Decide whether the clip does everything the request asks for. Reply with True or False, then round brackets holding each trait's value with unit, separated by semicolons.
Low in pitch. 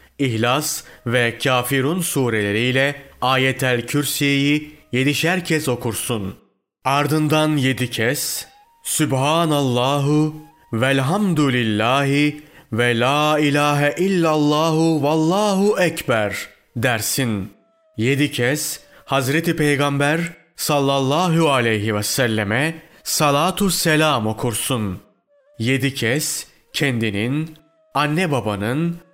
False (145 Hz)